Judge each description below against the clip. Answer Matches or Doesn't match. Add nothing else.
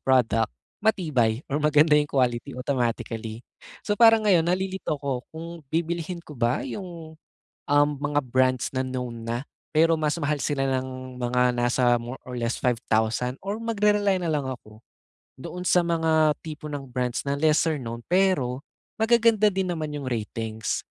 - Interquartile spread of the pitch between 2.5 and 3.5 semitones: Doesn't match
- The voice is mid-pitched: Matches